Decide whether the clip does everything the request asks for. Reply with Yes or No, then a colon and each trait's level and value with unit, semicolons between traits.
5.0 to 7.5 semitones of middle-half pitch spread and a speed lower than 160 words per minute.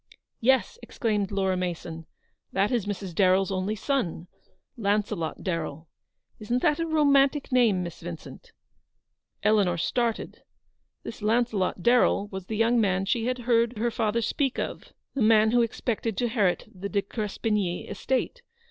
No: average, 4.1 semitones; average, 150 wpm